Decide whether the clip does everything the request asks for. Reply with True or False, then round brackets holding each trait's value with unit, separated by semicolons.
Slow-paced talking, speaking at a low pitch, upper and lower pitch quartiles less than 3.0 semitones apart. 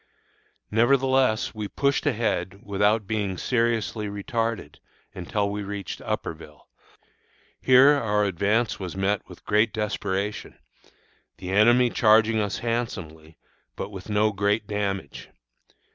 True (115 wpm; 105 Hz; 2.5 semitones)